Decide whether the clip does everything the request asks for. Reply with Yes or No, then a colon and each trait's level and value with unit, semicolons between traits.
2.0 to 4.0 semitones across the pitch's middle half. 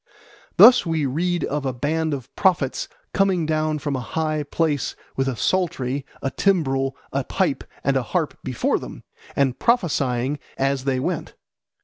Yes: average, 3.4 semitones